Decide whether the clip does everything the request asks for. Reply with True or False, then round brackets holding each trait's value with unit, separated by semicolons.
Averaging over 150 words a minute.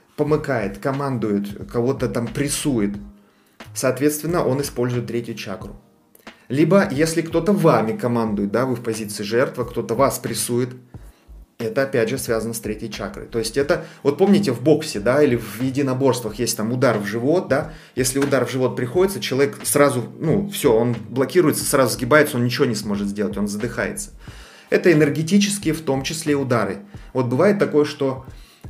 True (160 wpm)